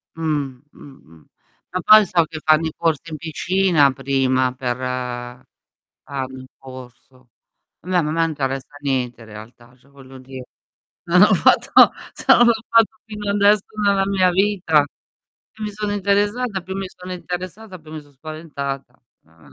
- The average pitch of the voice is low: No, medium, 155 Hz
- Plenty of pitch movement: Yes, wide, 6.5 semitones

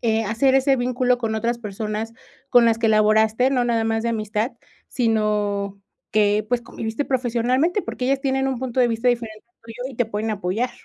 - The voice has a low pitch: No, high, 230 Hz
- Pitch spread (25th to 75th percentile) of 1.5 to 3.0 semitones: Yes, narrow, 2.5 semitones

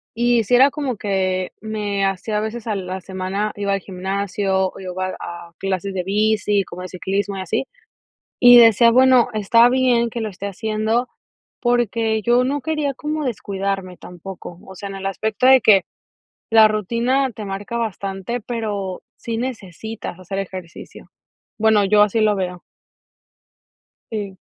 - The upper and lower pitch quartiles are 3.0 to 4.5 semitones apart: Yes, average, 3.4 semitones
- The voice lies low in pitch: No, high, 210 Hz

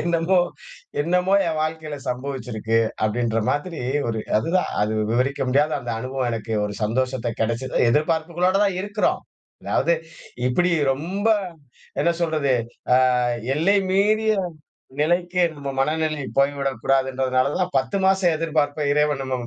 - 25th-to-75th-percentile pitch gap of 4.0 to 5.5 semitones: Yes, average, 4.9 semitones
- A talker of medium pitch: Yes, medium, 145 Hz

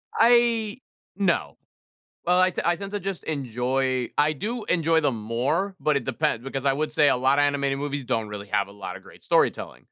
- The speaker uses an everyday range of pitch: No, wide, 6.2 semitones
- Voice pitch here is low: No, medium, 145 Hz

